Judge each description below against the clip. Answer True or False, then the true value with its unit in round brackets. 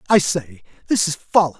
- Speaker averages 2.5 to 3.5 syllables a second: False (5.5 syllables/s)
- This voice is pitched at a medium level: True (160 Hz)